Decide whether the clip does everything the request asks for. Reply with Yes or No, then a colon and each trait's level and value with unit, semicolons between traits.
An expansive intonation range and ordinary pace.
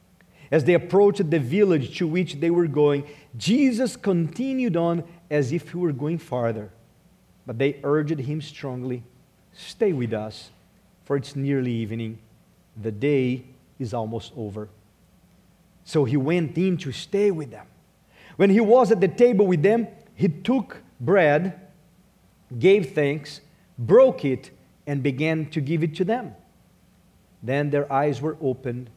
Yes: wide, 6.0 semitones; average, 145 wpm